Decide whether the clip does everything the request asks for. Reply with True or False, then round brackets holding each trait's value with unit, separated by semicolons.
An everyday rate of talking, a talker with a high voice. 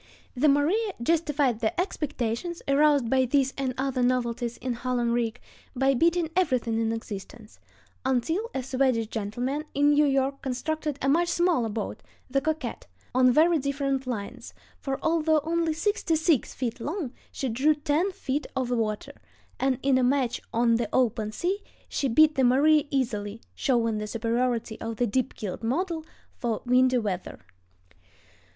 True (160 wpm; 260 Hz)